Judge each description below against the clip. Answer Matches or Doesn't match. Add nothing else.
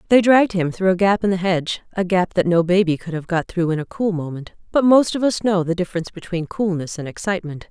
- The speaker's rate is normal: Doesn't match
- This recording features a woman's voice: Matches